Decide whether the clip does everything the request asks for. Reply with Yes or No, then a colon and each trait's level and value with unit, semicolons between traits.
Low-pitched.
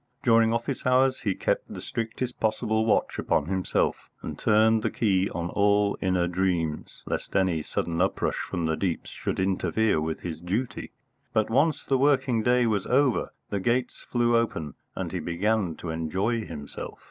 Yes: low, 105 Hz